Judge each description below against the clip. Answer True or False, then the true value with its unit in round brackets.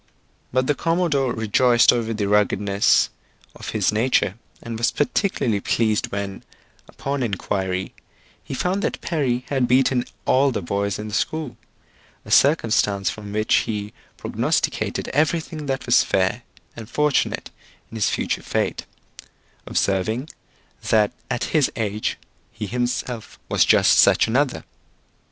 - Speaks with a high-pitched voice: False (115 Hz)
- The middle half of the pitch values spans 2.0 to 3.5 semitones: False (4.5 semitones)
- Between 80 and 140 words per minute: True (135 wpm)